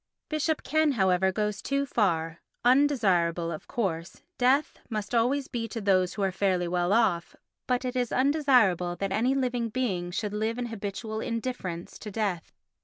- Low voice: No, high, 215 Hz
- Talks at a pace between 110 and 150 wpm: No, average, 165 wpm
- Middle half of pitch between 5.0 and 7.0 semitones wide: Yes, average, 5.3 semitones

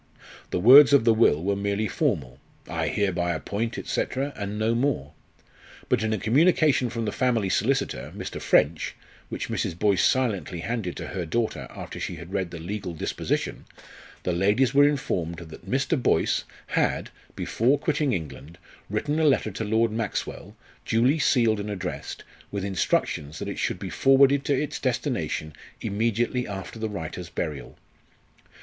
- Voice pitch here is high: No, low, 110 Hz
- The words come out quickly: No, average, 160 wpm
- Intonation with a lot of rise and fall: Yes, wide, 5.8 semitones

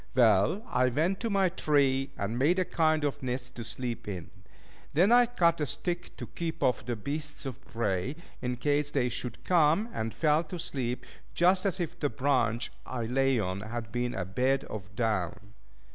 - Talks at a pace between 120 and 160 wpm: No, average, 190 wpm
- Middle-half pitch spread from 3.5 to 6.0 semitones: Yes, wide, 5.6 semitones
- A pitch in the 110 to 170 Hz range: Yes, low, 135 Hz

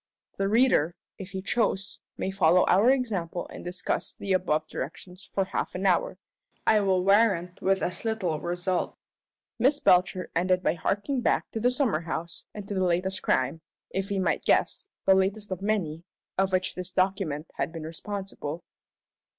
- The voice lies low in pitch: No, high, 190 Hz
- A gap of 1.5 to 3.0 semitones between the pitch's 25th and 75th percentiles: Yes, narrow, 2.4 semitones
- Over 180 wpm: No, average, 170 wpm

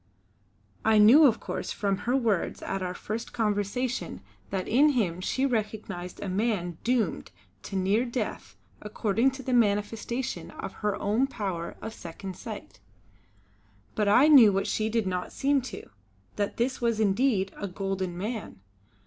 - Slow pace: No, average, 155 wpm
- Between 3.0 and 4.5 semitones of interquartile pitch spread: Yes, average, 3.8 semitones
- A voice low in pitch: No, high, 215 Hz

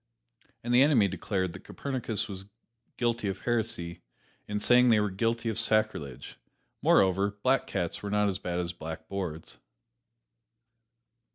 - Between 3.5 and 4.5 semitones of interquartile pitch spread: Yes, average, 4.0 semitones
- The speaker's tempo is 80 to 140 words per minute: Yes, slow, 135 wpm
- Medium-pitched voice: No, low, 105 Hz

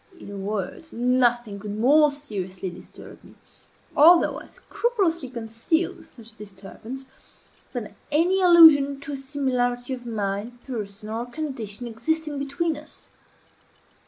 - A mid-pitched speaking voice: No, very high, 250 Hz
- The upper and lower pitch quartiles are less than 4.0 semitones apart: No, wide, 5.5 semitones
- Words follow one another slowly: Yes, slow, 125 wpm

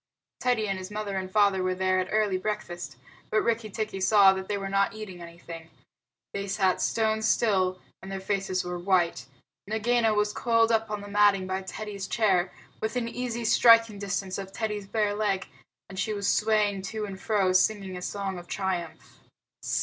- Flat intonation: Yes, narrow, 2.3 semitones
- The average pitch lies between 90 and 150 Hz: No, high, 200 Hz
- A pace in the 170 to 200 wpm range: Yes, average, 180 wpm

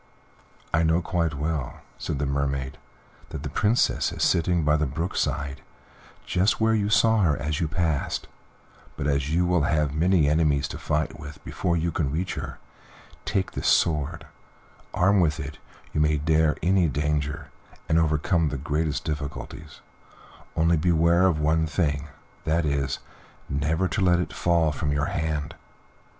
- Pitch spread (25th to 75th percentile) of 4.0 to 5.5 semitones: No, narrow, 2.6 semitones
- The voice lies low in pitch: Yes, very low, 80 Hz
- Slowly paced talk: No, average, 160 wpm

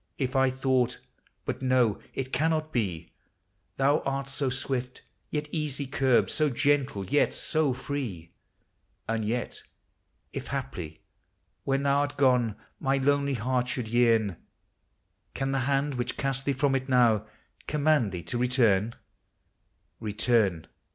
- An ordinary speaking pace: Yes, average, 145 wpm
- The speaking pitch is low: Yes, low, 130 Hz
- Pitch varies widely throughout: No, average, 3.1 semitones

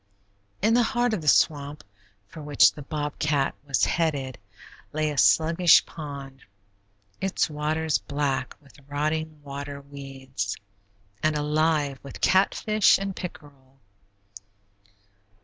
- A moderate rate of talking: No, slow, 115 wpm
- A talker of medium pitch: Yes, medium, 150 Hz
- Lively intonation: No, narrow, 2.4 semitones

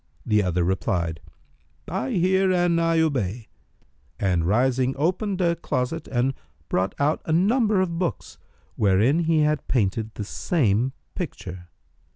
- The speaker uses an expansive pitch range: Yes, wide, 8.7 semitones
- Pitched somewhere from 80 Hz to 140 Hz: Yes, low, 135 Hz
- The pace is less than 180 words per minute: Yes, slow, 135 wpm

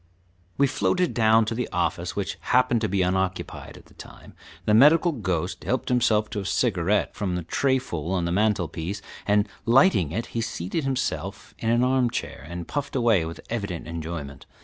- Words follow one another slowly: No, average, 180 wpm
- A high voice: No, low, 105 Hz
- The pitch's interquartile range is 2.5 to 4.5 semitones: No, wide, 5.6 semitones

